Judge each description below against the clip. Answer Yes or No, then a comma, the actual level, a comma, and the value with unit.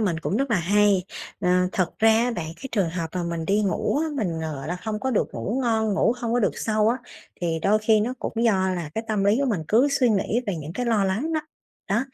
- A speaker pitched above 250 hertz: No, high, 210 Hz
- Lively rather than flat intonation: No, average, 4.2 semitones